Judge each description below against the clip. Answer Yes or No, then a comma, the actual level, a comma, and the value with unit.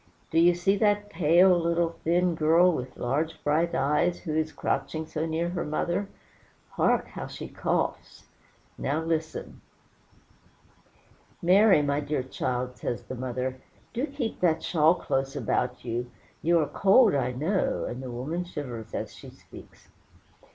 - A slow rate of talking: No, average, 150 wpm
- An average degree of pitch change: Yes, average, 4.8 semitones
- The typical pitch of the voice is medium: Yes, medium, 160 Hz